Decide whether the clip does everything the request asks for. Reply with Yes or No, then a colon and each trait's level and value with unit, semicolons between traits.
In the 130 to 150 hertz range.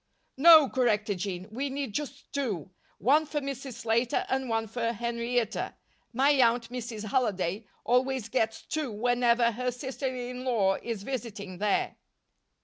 No: high, 240 Hz